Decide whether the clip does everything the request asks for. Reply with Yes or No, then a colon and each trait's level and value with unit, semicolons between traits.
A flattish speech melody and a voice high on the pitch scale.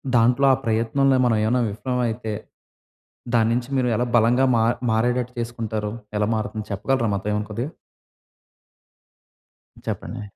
No: narrow, 2.2 semitones; low, 115 Hz